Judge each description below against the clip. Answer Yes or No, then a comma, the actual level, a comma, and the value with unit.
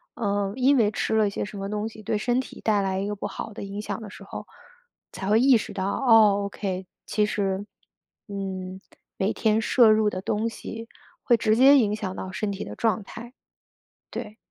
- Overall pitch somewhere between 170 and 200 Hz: No, high, 210 Hz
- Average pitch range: No, narrow, 2.1 semitones